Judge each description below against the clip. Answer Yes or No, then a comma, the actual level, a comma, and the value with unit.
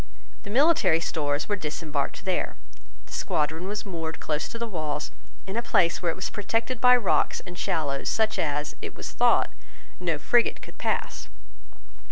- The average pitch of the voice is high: No, medium, 175 Hz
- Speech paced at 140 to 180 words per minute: Yes, average, 170 wpm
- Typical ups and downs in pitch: No, wide, 6.0 semitones